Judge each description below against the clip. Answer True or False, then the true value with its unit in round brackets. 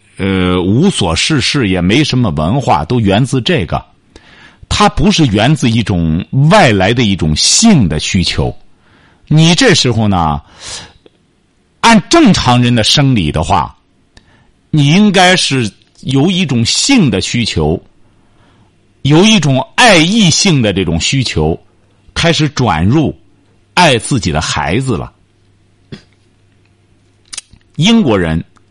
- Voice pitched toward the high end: False (105 Hz)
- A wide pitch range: True (7.7 semitones)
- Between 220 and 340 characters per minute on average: False (170 characters per minute)